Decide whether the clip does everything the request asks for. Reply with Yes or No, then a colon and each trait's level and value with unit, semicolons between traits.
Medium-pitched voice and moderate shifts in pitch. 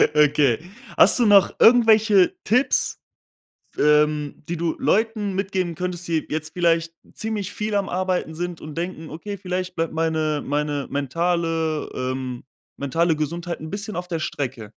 Yes: medium, 170 Hz; average, 3.7 semitones